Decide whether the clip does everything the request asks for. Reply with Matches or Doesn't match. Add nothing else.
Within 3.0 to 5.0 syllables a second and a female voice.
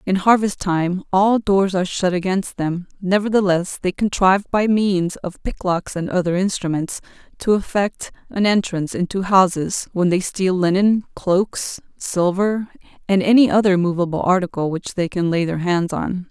Matches